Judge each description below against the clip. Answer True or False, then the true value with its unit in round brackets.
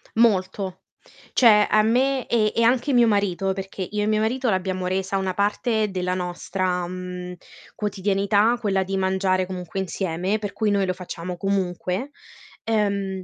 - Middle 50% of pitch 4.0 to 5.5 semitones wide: False (2.5 semitones)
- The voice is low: False (195 Hz)